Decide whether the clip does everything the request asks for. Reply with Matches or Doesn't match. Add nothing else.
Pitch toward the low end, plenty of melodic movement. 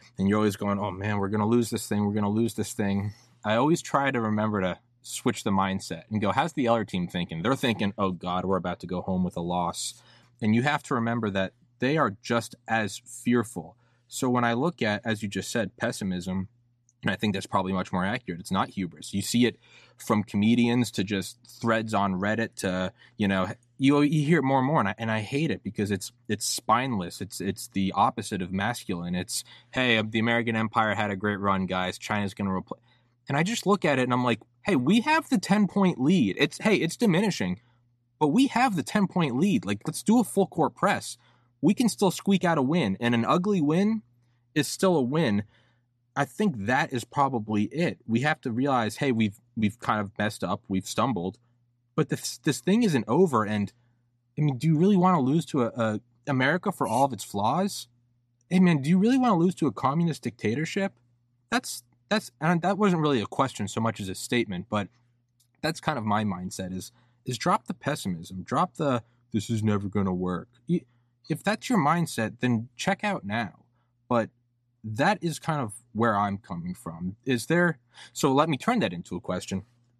Matches